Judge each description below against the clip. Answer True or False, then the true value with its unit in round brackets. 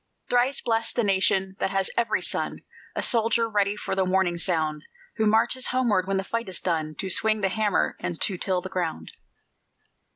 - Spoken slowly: False (190 wpm)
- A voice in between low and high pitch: False (195 Hz)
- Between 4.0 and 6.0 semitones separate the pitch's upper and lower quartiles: False (3.4 semitones)